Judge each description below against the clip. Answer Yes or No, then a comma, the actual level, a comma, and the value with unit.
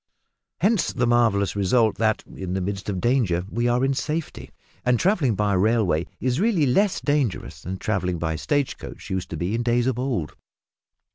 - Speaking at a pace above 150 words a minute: Yes, average, 185 wpm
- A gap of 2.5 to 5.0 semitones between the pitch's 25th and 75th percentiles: No, wide, 5.6 semitones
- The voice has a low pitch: Yes, low, 115 Hz